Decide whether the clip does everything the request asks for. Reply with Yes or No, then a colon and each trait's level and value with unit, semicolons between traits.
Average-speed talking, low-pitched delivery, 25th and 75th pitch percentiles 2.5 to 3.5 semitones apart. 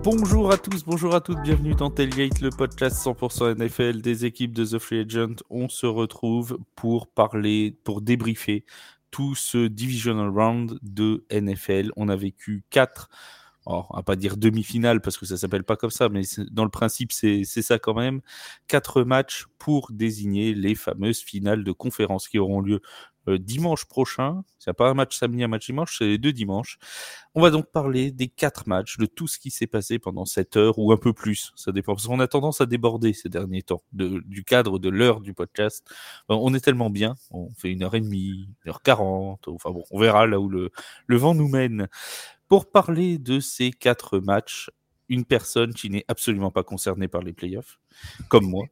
No: average, 200 wpm; low, 115 Hz; average, 4.1 semitones